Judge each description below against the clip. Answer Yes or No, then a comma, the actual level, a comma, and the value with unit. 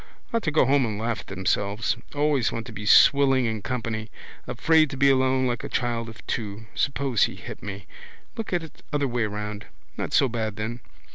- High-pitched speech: No, low, 120 Hz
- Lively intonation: No, average, 4.0 semitones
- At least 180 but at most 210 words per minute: Yes, fast, 205 wpm